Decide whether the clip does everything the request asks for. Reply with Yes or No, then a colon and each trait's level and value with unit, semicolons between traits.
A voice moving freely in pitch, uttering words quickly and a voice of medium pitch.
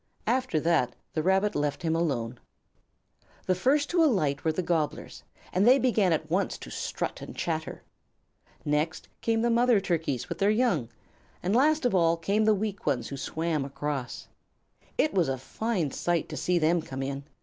No: wide, 6.4 semitones; average, 180 wpm; medium, 170 Hz